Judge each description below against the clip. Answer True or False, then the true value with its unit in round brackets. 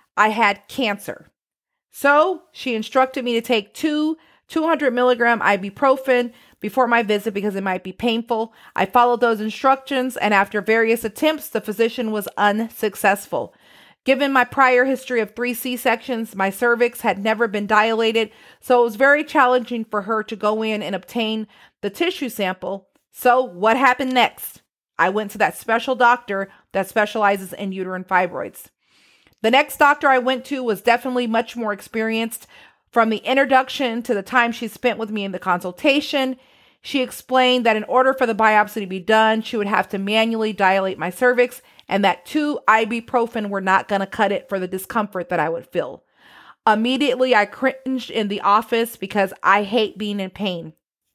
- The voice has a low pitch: False (225 Hz)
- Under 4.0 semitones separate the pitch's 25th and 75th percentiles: True (3.5 semitones)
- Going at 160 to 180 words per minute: True (175 wpm)